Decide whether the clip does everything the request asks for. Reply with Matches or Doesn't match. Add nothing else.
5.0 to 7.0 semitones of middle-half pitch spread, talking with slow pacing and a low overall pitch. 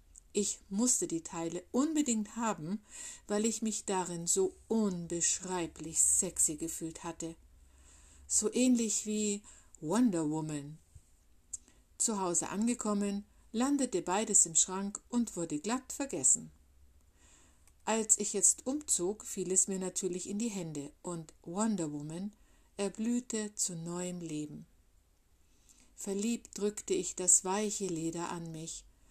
Doesn't match